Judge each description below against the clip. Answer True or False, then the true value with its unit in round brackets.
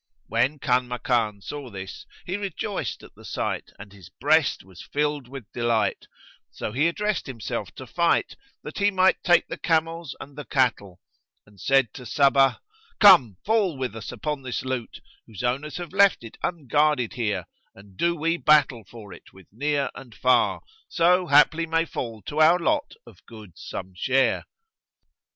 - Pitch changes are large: True (6.2 semitones)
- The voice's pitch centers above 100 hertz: True (135 Hz)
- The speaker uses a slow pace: False (165 wpm)